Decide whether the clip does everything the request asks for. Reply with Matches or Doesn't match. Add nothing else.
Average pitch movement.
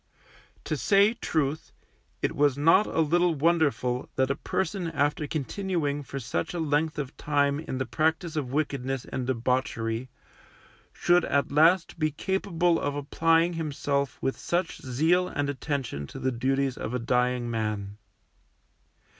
Matches